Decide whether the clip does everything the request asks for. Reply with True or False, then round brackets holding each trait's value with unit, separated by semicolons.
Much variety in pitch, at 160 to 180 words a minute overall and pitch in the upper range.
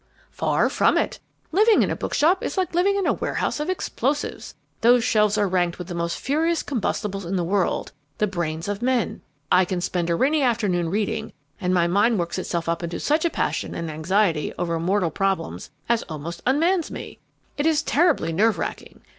False (8.4 semitones; 195 wpm; 205 Hz)